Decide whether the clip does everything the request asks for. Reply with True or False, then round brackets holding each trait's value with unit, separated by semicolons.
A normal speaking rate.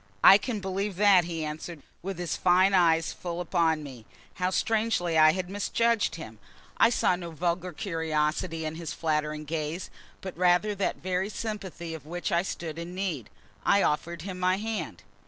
True (175 wpm)